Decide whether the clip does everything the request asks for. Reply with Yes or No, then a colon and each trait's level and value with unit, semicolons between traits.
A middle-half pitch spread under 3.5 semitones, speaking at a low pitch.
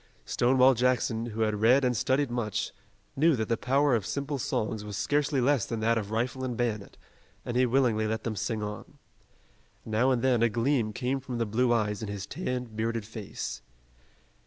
Yes: average, 2.8 semitones; low, 120 Hz